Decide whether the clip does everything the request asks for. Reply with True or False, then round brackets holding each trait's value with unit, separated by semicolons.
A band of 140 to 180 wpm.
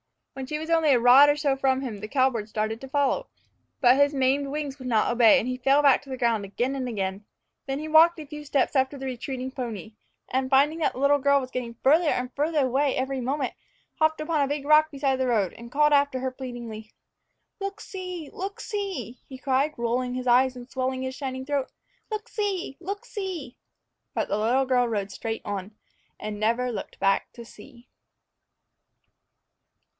False (200 wpm)